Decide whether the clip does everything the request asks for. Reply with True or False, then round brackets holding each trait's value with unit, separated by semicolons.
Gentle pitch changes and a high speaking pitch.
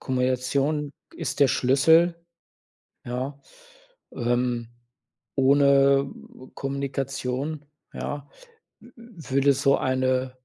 False (1.8 semitones; 135 Hz)